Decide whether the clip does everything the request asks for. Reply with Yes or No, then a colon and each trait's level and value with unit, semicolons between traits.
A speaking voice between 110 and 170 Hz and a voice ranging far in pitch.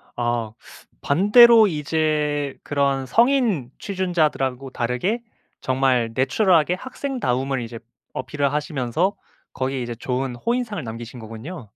Yes: medium, 140 Hz; wide, 6.6 semitones